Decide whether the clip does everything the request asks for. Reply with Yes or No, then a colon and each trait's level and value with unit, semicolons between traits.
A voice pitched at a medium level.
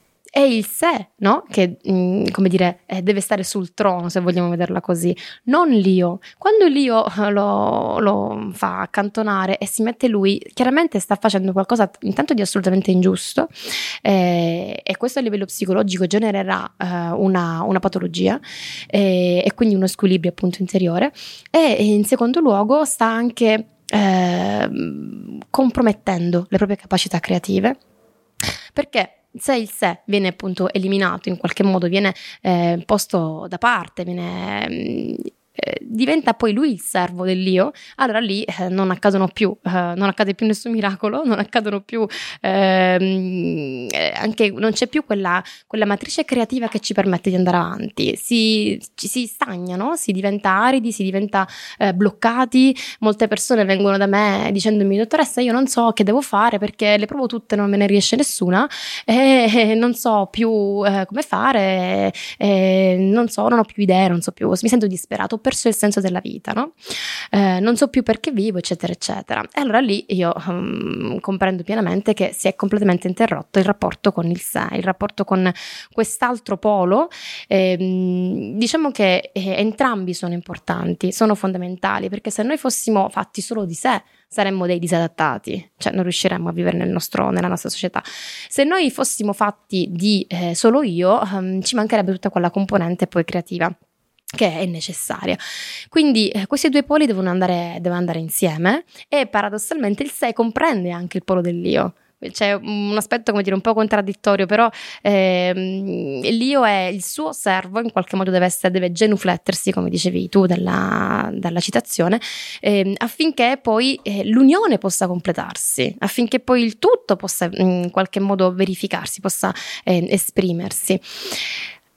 No: high, 200 Hz